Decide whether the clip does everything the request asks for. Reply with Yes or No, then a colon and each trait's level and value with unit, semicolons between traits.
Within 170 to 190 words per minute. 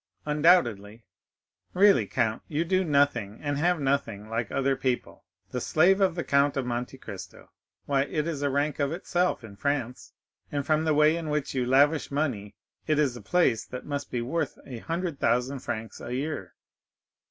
Yes: average, 180 wpm